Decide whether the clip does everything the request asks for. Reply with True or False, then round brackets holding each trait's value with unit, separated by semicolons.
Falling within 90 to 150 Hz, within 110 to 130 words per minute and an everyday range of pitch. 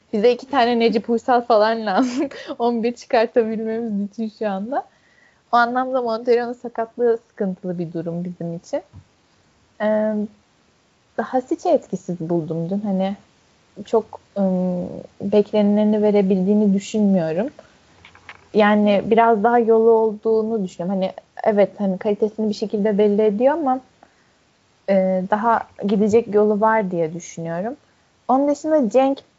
False (220 Hz; 120 wpm; 3.0 semitones)